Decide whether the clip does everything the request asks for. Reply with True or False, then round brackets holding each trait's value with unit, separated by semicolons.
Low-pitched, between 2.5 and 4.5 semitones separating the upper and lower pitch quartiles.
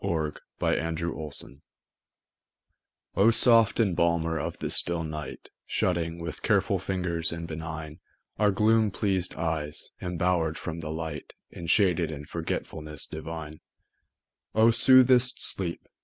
True (85 Hz; 3.3 semitones)